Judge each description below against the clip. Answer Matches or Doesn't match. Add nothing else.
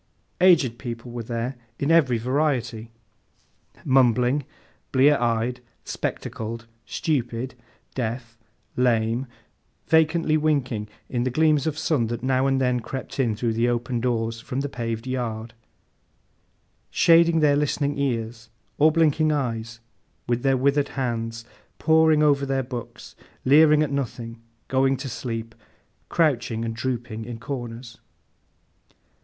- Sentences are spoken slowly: Matches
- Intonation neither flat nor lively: Matches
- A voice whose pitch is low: Matches